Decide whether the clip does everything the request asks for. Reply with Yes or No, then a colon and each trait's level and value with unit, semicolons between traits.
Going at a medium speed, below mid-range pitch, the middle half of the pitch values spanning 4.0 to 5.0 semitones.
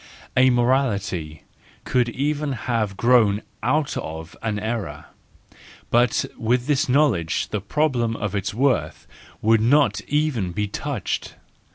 No: slow, 125 wpm; low, 120 Hz; average, 4.3 semitones